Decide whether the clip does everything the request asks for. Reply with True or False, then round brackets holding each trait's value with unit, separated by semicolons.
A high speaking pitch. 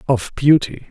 False (140 Hz)